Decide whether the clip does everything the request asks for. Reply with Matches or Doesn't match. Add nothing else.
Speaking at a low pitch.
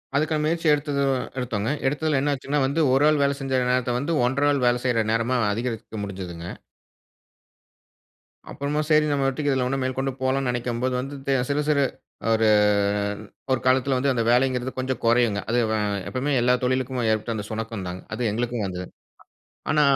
Matches